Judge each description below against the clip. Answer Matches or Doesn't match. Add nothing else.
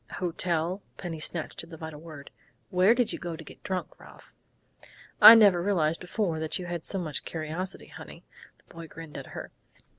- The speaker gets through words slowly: Doesn't match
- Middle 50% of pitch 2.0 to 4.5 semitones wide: Matches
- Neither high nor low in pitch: Matches